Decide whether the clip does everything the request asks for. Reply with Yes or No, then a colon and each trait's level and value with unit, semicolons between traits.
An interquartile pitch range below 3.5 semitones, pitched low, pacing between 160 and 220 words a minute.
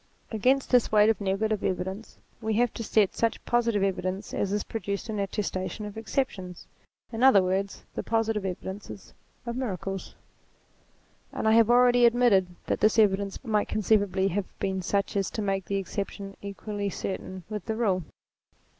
No: narrow, 2.5 semitones; high, 205 Hz; average, 165 wpm